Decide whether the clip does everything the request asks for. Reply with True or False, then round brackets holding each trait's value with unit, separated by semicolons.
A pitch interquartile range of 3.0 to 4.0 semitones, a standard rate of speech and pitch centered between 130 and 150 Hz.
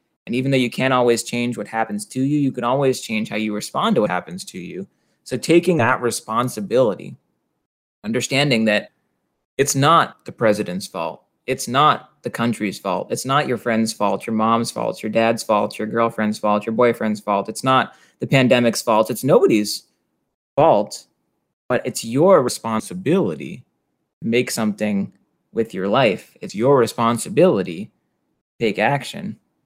False (3.3 semitones; 160 wpm; 115 Hz)